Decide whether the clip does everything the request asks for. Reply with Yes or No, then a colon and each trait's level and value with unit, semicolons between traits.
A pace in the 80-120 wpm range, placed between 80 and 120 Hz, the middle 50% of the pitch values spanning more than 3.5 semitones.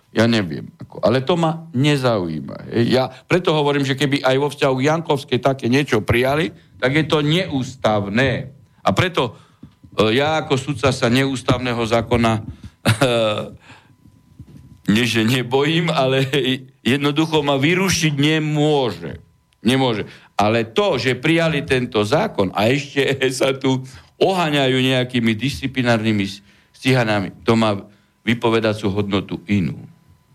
No: average, 115 wpm; low, 130 Hz; average, 4.0 semitones